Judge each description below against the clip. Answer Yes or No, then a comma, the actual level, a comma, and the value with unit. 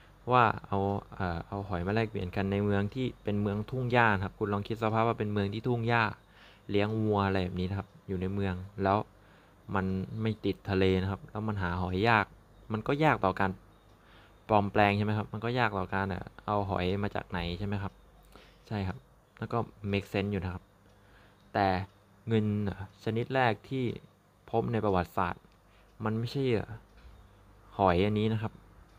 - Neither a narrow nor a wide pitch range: No, narrow, 2.3 semitones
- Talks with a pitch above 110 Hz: No, low, 100 Hz